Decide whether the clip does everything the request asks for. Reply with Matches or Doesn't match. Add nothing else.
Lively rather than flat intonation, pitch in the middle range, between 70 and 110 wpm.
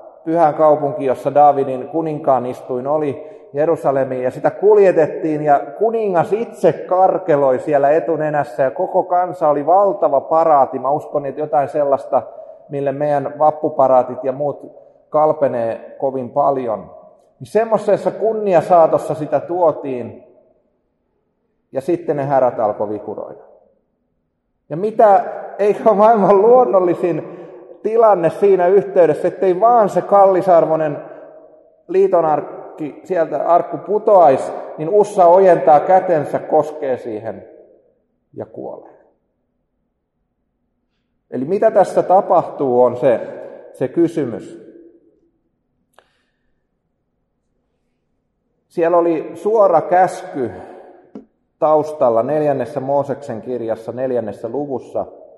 Matches